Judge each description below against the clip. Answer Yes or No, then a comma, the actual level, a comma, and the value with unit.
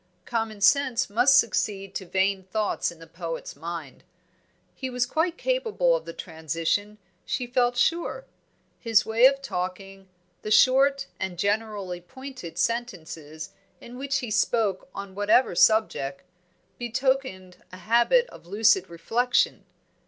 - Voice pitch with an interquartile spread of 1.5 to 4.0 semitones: No, wide, 5.5 semitones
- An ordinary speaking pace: No, slow, 130 wpm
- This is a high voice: Yes, high, 215 Hz